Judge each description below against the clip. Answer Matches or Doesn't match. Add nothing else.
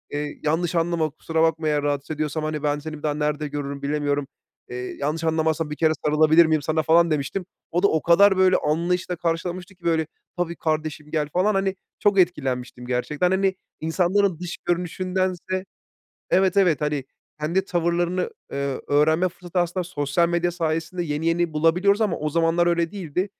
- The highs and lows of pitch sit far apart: Doesn't match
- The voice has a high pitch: Doesn't match